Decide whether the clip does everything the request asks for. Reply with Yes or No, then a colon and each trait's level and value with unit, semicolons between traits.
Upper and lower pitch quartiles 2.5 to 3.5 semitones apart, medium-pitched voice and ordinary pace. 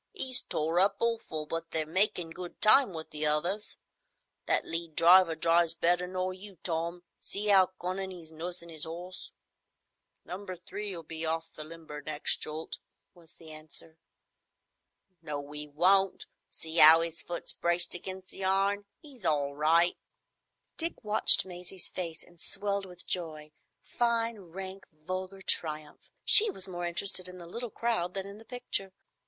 Yes: average, 3.0 semitones; medium, 175 Hz; average, 155 wpm